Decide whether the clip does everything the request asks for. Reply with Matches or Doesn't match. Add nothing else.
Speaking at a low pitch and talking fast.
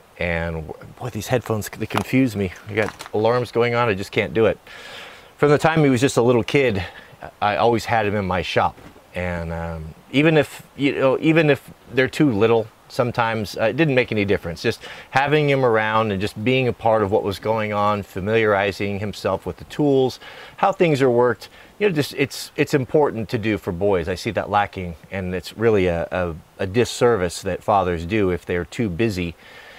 Matches